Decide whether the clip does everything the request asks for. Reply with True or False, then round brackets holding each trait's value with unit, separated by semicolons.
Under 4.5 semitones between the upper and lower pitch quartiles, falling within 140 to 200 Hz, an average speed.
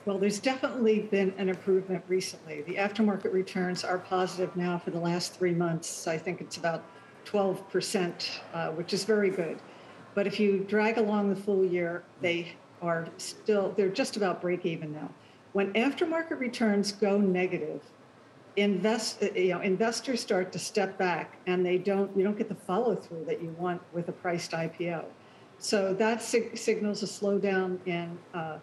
True (2.8 semitones; 190 Hz; 175 wpm)